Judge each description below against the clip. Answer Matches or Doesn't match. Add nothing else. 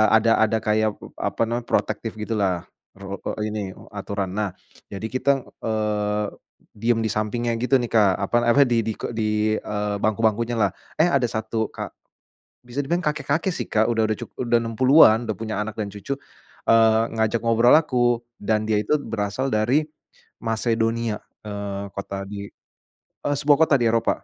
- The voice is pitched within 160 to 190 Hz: Doesn't match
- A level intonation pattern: Matches